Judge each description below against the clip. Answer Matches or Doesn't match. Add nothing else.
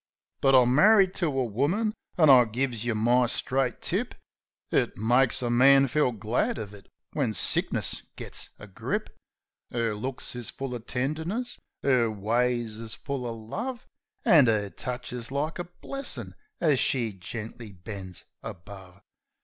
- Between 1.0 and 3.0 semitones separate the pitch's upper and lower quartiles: Doesn't match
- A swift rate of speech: Doesn't match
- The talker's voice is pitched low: Matches